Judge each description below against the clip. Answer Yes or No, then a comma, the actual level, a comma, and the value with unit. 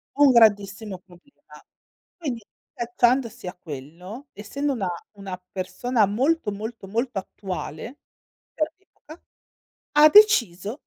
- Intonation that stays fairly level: No, wide, 5.9 semitones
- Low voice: No, high, 220 Hz